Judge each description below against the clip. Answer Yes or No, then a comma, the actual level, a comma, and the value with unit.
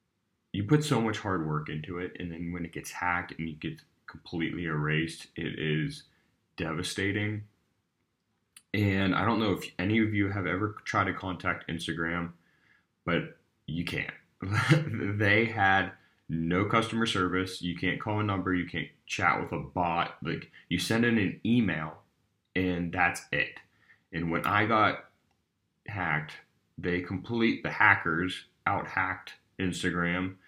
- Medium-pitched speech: No, very low, 95 Hz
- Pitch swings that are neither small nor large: Yes, average, 3.5 semitones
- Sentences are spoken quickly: No, average, 150 wpm